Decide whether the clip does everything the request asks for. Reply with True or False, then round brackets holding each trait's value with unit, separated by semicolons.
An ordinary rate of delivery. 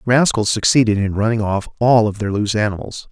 False (210 wpm)